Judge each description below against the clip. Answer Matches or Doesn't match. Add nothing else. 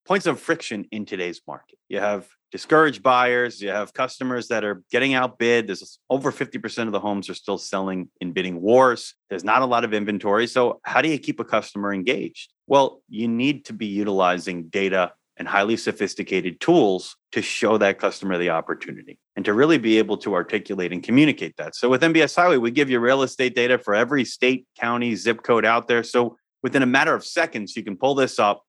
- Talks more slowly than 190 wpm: Doesn't match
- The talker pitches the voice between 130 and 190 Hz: Doesn't match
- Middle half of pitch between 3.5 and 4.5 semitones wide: Matches